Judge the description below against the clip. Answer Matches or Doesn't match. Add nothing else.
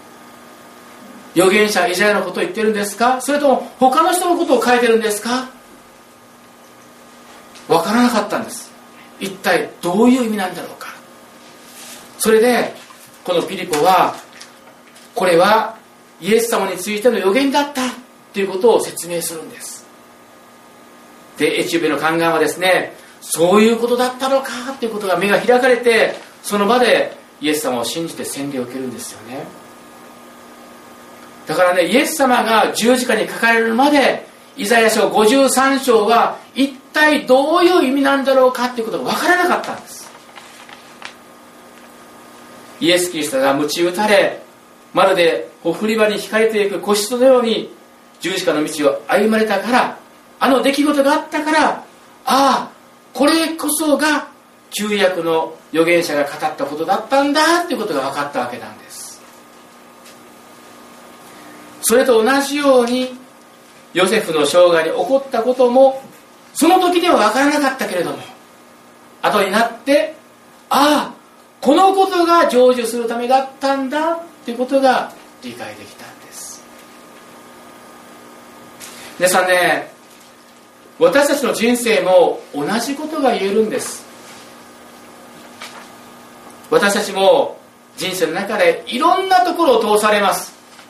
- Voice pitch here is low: Doesn't match